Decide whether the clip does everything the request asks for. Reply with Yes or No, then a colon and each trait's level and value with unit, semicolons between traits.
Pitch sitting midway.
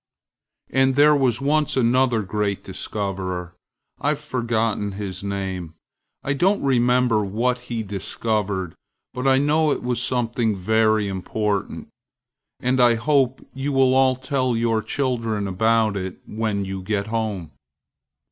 No: low, 115 Hz